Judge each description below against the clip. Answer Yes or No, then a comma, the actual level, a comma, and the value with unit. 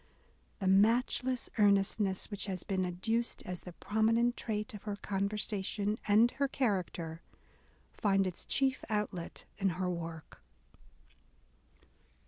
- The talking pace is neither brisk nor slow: No, slow, 115 wpm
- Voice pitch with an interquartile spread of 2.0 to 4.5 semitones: Yes, average, 3.0 semitones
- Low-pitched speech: No, high, 200 Hz